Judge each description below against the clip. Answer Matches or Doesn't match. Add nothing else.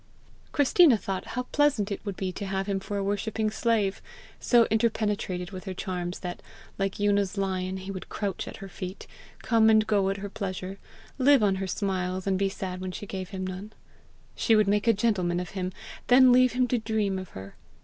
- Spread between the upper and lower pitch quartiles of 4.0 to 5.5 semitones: Doesn't match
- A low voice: Doesn't match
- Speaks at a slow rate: Doesn't match